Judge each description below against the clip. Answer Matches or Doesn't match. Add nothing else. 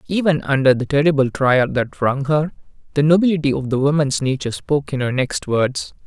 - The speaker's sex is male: Matches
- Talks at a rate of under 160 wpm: Doesn't match